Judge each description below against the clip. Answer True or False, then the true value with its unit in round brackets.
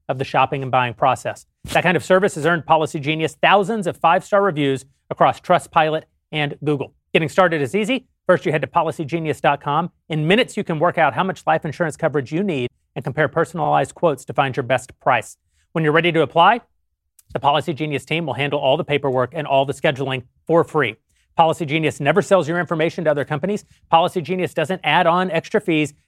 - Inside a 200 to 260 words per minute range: True (205 wpm)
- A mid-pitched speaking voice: True (160 Hz)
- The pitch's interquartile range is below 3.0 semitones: False (3.4 semitones)